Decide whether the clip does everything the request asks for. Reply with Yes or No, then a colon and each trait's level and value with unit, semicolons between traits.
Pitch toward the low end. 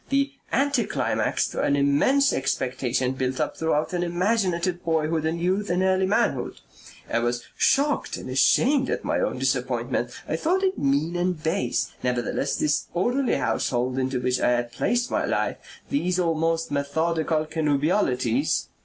No: medium, 165 Hz